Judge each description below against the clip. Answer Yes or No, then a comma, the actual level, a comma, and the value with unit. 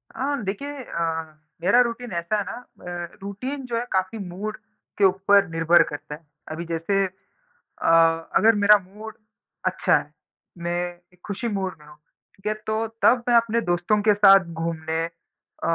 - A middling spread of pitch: Yes, average, 4.3 semitones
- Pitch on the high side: Yes, high, 195 Hz